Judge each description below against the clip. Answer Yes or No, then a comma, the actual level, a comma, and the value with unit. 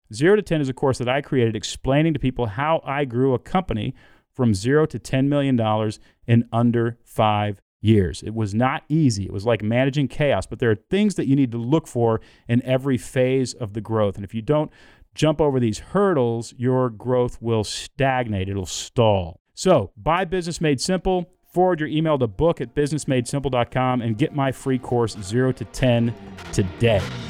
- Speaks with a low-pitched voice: Yes, low, 125 Hz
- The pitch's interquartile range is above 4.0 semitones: Yes, average, 4.5 semitones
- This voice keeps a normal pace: Yes, average, 190 wpm